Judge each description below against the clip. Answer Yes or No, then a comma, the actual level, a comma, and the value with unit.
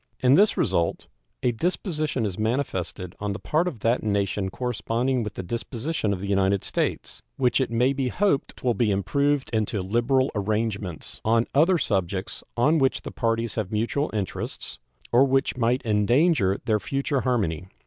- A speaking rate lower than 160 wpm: No, average, 165 wpm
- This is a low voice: Yes, low, 115 Hz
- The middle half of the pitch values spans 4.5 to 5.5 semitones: Yes, average, 4.9 semitones